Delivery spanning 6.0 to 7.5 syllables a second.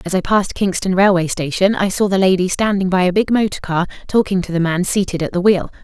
Yes: 6.1 syllables/s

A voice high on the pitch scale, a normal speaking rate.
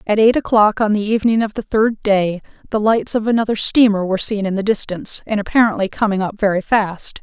No: high, 210 Hz; fast, 215 wpm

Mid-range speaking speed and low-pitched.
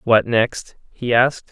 Yes: average, 160 wpm; low, 120 Hz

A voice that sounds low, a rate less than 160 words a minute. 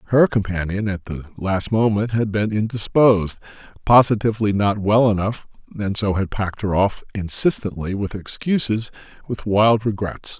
Yes: low, 105 Hz; average, 140 wpm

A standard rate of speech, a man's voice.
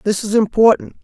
Yes: average, 175 wpm; male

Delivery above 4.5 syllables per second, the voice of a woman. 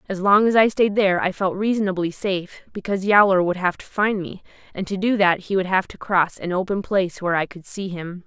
Yes: 5.9 syllables/s; female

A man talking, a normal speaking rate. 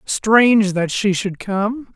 Yes: male; average, 155 wpm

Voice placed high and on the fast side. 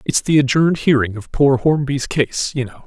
No: low, 135 Hz; fast, 210 wpm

